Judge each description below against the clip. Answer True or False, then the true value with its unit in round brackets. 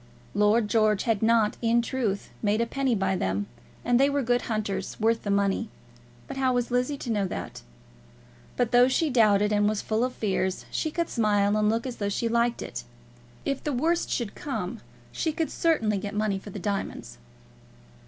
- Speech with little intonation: False (3.3 semitones)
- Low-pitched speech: False (225 Hz)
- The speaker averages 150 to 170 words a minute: False (195 wpm)